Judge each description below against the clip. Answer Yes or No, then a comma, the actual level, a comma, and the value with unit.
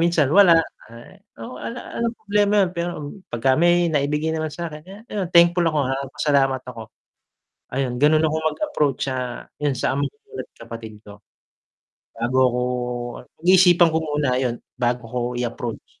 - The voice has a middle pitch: Yes, medium, 150 Hz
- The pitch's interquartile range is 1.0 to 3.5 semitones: No, wide, 5.4 semitones